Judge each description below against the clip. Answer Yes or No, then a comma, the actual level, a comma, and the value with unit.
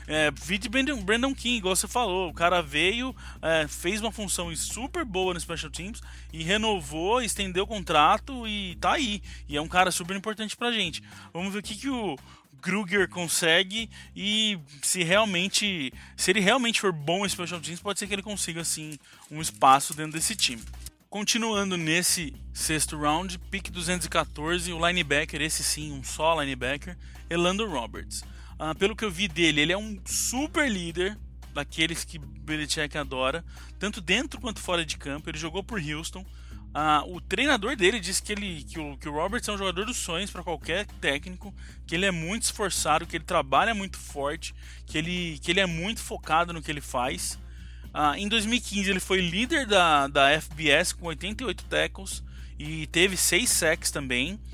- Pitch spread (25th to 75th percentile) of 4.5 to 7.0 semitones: Yes, average, 5.1 semitones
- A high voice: No, medium, 175 Hz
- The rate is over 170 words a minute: Yes, average, 180 wpm